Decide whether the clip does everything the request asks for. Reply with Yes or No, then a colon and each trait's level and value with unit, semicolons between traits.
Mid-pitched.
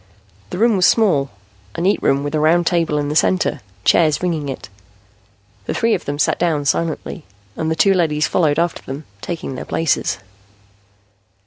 Yes: medium, 160 Hz